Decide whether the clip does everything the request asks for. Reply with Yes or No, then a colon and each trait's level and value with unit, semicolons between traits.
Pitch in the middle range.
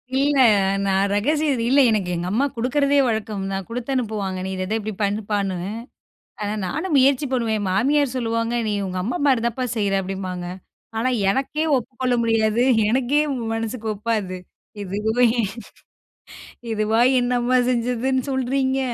No: high, 230 Hz